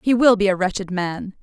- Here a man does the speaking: No, female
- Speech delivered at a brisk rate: Yes, fast, 255 wpm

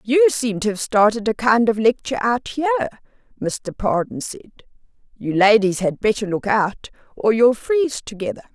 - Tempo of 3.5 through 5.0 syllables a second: No, 5.2 syllables/s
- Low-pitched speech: No, high, 225 Hz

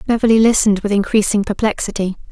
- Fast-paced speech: No, slow, 130 wpm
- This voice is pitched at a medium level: No, high, 210 Hz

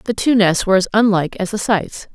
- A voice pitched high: Yes, high, 200 Hz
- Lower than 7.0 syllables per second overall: Yes, 6.4 syllables/s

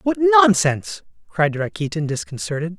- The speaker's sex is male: Yes, male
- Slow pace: Yes, slow, 110 wpm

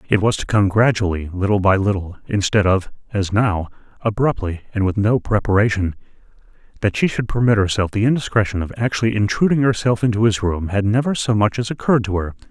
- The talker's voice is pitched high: No, low, 105 Hz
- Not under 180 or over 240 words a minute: Yes, average, 185 wpm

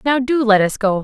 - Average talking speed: No, fast, 290 wpm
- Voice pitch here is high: Yes, high, 230 Hz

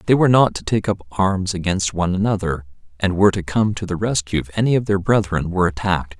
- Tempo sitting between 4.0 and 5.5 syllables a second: No, 6.4 syllables/s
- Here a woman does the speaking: No, male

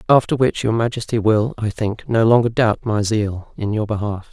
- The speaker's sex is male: Yes, male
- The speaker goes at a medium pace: No, fast, 210 wpm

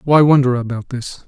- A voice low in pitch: Yes, low, 130 Hz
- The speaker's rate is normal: Yes, average, 190 wpm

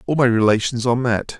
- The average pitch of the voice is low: Yes, low, 120 Hz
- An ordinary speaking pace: No, fast, 215 wpm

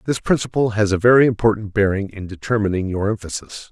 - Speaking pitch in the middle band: No, low, 105 Hz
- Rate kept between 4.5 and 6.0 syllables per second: No, 6.2 syllables/s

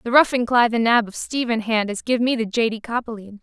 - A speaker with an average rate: No, fast, 245 wpm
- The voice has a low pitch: No, high, 230 Hz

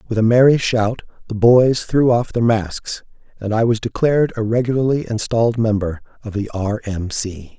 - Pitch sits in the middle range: No, low, 115 Hz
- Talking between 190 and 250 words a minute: No, average, 180 wpm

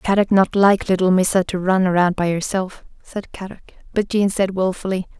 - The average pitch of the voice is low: No, high, 190 Hz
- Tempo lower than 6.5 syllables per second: Yes, 5.1 syllables/s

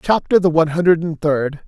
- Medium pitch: Yes, medium, 165 Hz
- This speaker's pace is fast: Yes, fast, 215 wpm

